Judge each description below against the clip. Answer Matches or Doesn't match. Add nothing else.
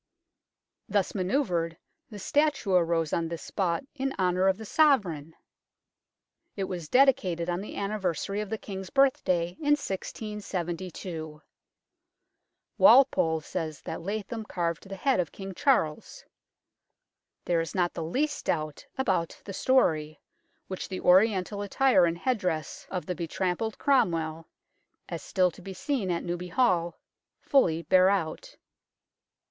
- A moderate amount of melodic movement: Matches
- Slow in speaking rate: Matches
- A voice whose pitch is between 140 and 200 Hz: Matches